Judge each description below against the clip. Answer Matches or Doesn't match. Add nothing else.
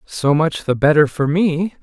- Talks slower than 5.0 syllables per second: Matches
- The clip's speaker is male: Matches